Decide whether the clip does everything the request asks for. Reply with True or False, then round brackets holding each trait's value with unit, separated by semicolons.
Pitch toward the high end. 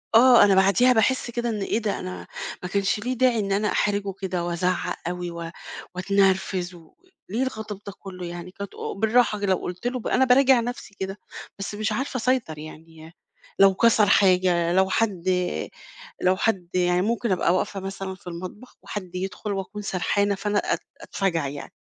True (195 Hz)